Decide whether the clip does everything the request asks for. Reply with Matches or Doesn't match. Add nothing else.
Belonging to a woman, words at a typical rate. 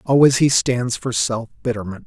Doesn't match